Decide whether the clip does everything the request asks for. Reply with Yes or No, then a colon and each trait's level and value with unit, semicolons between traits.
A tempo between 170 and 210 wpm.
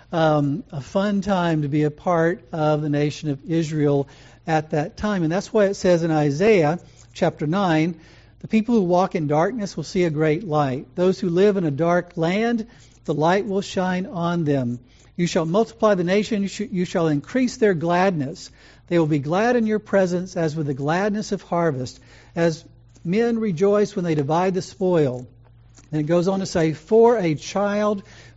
Yes: average, 195 wpm